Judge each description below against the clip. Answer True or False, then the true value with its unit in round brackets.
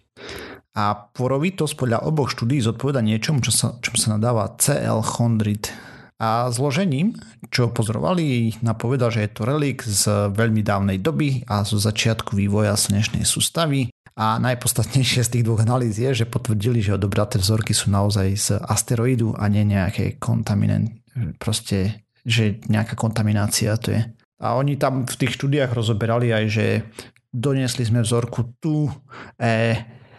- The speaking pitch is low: True (115 Hz)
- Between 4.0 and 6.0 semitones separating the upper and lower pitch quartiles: False (2.8 semitones)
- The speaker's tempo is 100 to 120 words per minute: False (145 wpm)